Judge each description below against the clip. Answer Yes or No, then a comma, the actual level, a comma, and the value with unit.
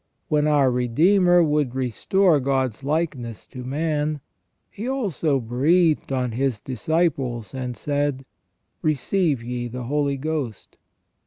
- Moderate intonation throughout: Yes, average, 3.9 semitones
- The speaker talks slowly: Yes, slow, 125 wpm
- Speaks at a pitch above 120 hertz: Yes, medium, 140 Hz